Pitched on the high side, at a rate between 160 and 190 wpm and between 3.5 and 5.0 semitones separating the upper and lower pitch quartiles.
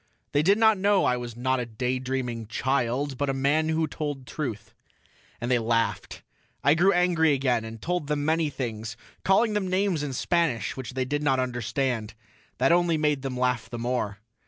No: low, 135 Hz; average, 185 wpm; average, 4.6 semitones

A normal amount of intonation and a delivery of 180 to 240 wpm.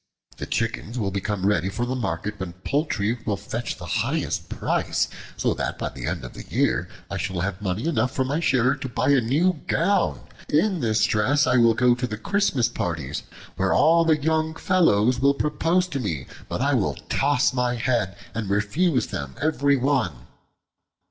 No: wide, 6.2 semitones; average, 190 wpm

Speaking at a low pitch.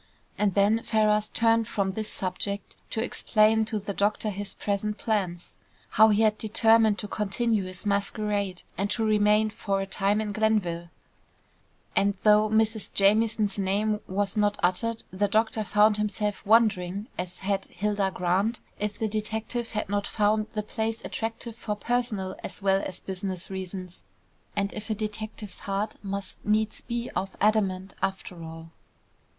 No: high, 210 Hz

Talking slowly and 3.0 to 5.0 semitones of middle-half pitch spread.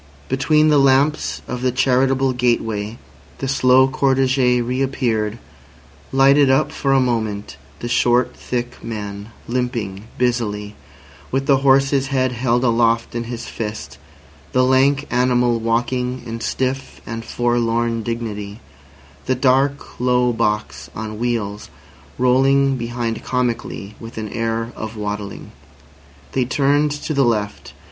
No: slow, 125 wpm; narrow, 2.6 semitones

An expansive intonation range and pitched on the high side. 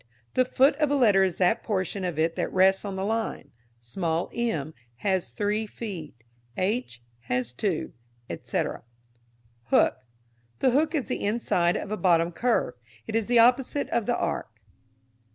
Yes: wide, 5.9 semitones; high, 195 Hz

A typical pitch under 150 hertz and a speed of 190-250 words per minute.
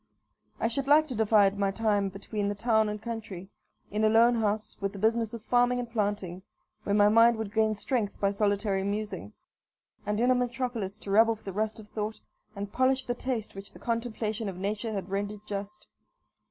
No: high, 215 Hz; average, 200 wpm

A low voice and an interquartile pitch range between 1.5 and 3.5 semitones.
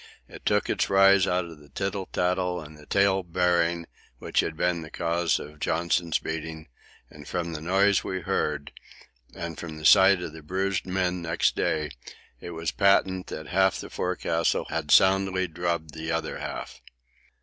Yes: very low, 85 Hz; average, 2.7 semitones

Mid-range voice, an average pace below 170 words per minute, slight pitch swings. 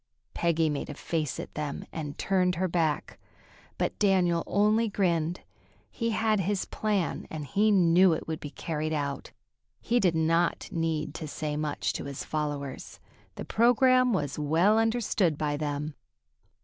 No: medium, 165 Hz; average, 155 wpm; average, 4.8 semitones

